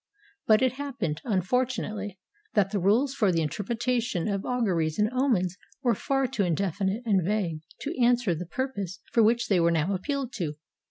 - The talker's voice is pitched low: No, high, 210 Hz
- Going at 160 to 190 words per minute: Yes, average, 175 wpm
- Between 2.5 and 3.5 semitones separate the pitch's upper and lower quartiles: No, wide, 5.4 semitones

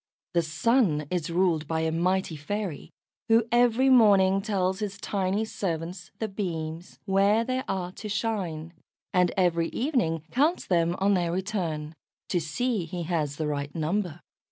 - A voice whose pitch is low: No, medium, 185 Hz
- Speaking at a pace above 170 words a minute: No, average, 155 wpm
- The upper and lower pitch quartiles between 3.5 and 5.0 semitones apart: Yes, average, 4.2 semitones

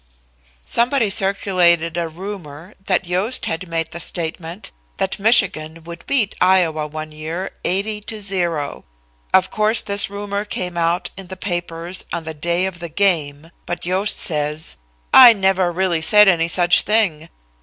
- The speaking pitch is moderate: Yes, medium, 180 Hz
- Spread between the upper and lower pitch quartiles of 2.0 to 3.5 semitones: Yes, average, 3.2 semitones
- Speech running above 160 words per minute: No, average, 155 wpm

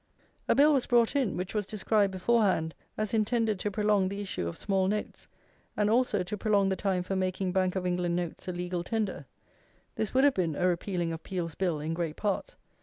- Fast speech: Yes, fast, 210 wpm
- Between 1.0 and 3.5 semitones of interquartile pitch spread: Yes, average, 3.0 semitones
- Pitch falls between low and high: No, high, 195 Hz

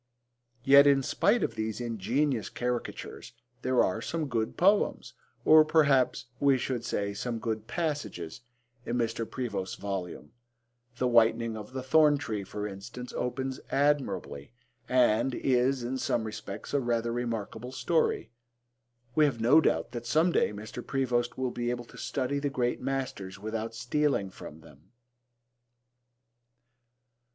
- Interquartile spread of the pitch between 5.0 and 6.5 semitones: No, average, 3.6 semitones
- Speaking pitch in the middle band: No, low, 120 Hz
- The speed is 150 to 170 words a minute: No, average, 140 wpm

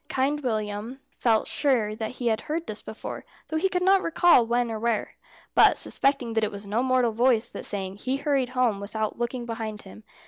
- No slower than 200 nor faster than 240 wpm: Yes, fast, 205 wpm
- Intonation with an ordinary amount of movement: Yes, average, 3.5 semitones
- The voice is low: No, high, 235 Hz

